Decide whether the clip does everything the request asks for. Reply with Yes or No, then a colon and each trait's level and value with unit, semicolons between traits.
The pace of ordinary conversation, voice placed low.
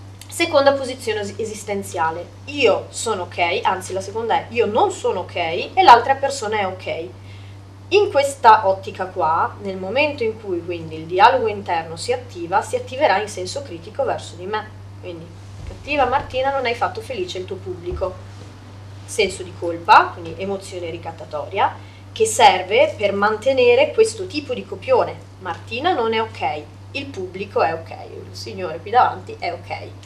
No: average, 160 wpm; high, 210 Hz